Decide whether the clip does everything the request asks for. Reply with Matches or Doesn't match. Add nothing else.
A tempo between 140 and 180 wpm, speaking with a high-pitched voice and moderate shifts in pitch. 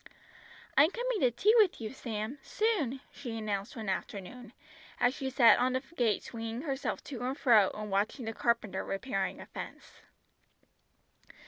Matches